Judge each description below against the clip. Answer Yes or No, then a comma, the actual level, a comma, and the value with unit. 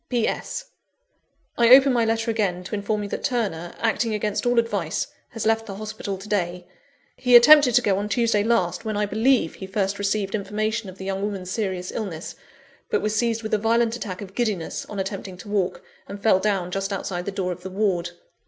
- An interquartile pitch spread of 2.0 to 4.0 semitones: Yes, average, 2.9 semitones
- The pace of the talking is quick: Yes, fast, 210 wpm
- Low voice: No, high, 205 Hz